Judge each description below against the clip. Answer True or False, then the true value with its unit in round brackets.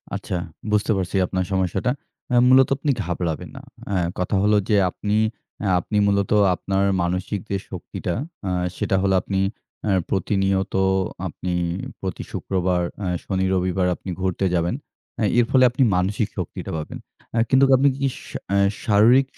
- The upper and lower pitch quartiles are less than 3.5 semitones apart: True (2.5 semitones)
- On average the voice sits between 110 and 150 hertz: False (95 Hz)